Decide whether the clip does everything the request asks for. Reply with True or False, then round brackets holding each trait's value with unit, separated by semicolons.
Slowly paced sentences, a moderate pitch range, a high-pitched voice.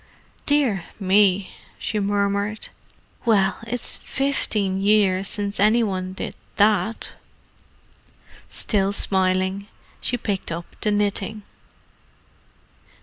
False (90 wpm; 1.9 semitones; 200 Hz)